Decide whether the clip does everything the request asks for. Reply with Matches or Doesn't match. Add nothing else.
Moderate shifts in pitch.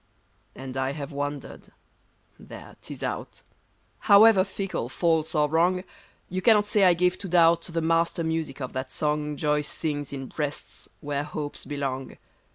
Matches